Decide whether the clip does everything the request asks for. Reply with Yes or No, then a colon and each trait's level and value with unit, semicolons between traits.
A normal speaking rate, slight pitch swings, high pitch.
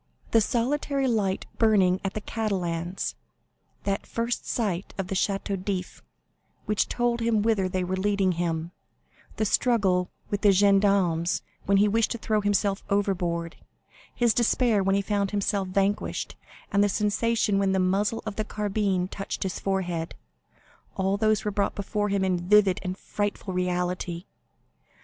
Yes: average, 150 wpm; narrow, 2.3 semitones; high, 200 Hz